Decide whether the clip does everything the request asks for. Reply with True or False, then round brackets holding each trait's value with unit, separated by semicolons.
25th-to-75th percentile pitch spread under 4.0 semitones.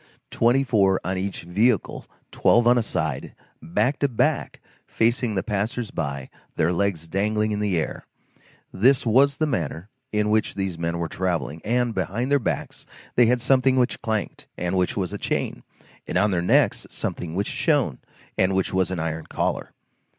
False (5.4 semitones)